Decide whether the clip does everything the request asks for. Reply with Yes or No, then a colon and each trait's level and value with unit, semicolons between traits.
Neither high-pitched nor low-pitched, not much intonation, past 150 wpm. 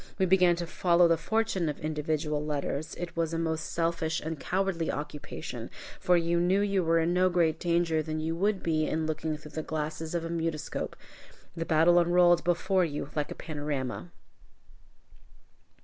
Yes: medium, 165 Hz; narrow, 2.0 semitones; average, 175 wpm